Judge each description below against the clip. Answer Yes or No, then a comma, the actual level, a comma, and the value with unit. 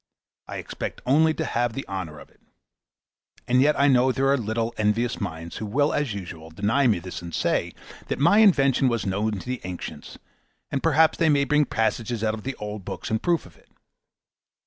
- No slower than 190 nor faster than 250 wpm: Yes, fast, 205 wpm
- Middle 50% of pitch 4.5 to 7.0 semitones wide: Yes, wide, 5.5 semitones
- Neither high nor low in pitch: No, low, 120 Hz